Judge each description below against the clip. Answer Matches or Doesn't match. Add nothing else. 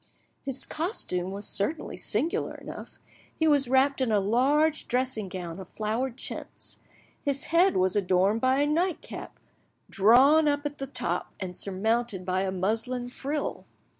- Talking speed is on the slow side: Doesn't match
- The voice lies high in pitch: Matches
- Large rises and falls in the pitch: Matches